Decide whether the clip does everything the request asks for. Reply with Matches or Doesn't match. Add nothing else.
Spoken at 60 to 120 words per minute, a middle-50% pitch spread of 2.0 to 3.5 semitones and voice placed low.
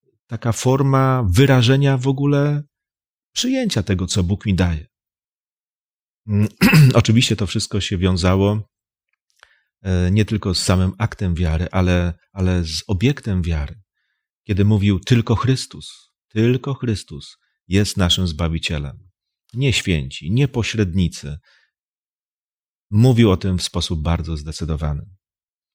Doesn't match